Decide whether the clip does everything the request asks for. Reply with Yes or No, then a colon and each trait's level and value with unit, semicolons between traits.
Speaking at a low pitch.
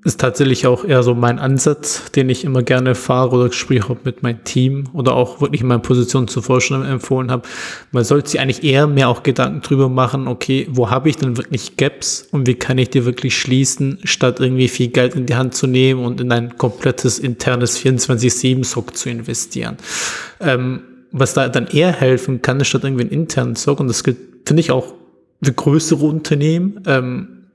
Yes: low, 130 Hz